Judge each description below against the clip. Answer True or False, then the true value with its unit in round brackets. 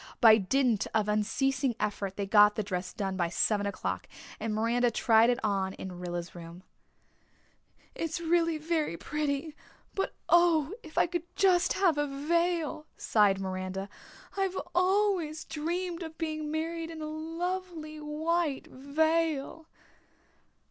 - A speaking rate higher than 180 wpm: False (135 wpm)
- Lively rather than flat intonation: True (7.8 semitones)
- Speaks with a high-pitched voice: True (300 Hz)